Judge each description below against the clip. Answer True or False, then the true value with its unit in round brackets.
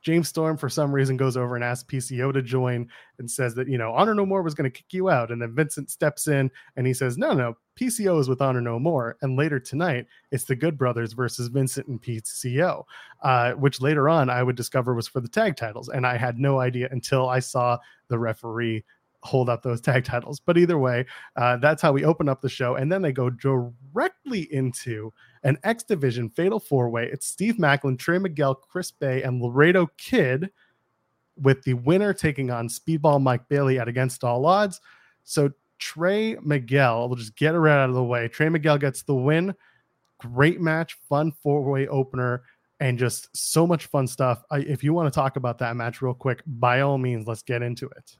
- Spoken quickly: True (215 wpm)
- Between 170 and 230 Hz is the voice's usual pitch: False (135 Hz)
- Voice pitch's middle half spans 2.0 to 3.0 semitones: False (3.7 semitones)